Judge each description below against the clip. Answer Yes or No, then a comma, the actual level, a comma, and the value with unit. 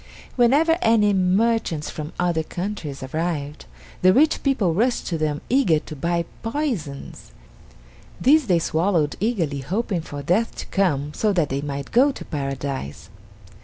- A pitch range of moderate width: No, wide, 7.3 semitones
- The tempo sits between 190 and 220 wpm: No, average, 145 wpm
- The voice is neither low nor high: Yes, medium, 175 Hz